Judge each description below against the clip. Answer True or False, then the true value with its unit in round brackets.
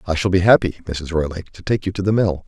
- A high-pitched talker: False (90 Hz)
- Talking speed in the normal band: False (290 wpm)